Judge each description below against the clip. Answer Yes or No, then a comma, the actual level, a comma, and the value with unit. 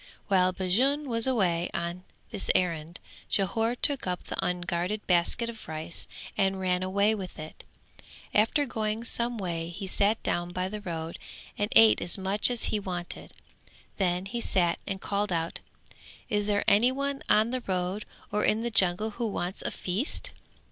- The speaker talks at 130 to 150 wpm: No, average, 165 wpm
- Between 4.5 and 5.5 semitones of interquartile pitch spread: No, average, 3.7 semitones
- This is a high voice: Yes, high, 195 Hz